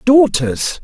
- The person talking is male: No, female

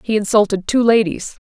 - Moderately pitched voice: No, high, 210 Hz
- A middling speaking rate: Yes, average, 165 wpm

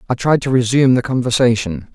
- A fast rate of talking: No, average, 185 wpm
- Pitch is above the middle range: No, low, 120 Hz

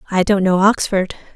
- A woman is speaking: Yes, female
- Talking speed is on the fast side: No, average, 175 wpm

